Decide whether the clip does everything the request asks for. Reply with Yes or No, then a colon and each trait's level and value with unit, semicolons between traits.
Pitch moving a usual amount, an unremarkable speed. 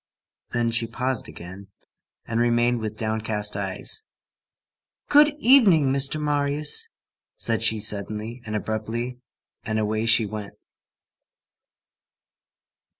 No: average, 3.6 semitones; slow, 100 wpm